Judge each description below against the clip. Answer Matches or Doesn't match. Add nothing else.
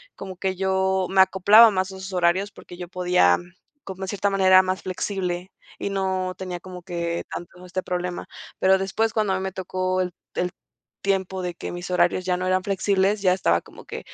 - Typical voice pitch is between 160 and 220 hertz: Matches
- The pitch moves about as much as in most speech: Doesn't match